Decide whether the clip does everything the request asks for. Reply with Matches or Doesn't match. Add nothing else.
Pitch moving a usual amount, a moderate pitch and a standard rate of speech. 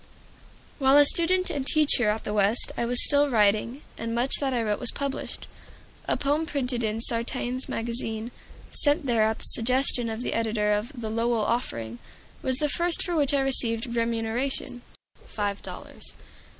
Doesn't match